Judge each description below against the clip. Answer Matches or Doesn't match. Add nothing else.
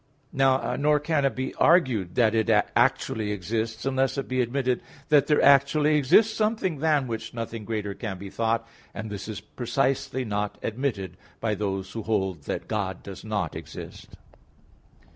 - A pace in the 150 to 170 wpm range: Matches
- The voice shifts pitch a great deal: Doesn't match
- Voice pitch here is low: Matches